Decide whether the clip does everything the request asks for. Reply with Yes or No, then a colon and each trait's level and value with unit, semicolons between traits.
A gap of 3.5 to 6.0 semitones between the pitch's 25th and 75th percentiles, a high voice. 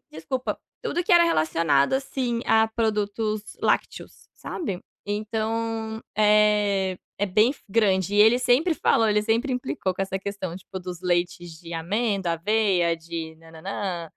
Yes: average, 4.1 semitones; high, 205 Hz